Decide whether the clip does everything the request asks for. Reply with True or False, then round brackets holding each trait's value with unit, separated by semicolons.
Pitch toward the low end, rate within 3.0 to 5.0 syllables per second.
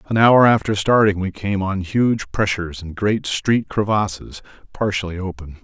True (100 Hz; 4.5 syllables/s)